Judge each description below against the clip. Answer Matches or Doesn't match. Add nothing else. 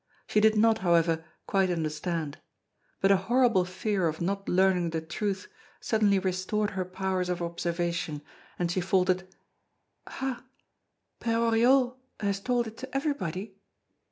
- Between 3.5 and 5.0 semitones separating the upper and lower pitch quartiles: Matches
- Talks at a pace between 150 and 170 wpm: Doesn't match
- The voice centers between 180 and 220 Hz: Matches